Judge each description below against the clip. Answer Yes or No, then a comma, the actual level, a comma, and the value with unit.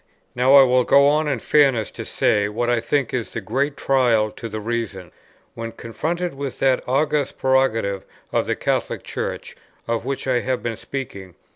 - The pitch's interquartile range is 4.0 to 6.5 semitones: No, average, 3.3 semitones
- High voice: No, low, 125 Hz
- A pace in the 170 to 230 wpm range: Yes, average, 180 wpm